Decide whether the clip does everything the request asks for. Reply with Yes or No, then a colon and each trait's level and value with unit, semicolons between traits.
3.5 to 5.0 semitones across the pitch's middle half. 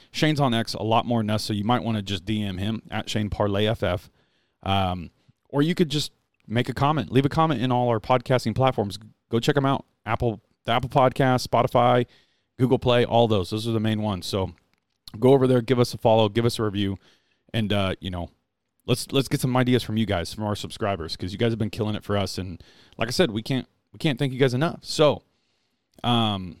Yes: average, 3.8 semitones